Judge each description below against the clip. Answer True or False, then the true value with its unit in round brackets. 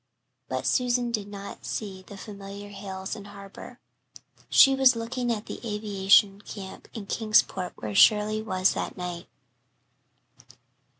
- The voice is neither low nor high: False (205 Hz)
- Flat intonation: True (2.3 semitones)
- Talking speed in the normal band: False (130 wpm)